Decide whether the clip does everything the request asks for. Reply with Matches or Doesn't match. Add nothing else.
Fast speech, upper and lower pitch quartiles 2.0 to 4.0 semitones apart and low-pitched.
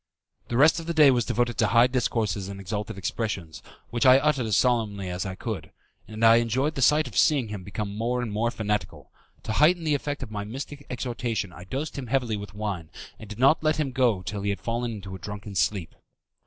Doesn't match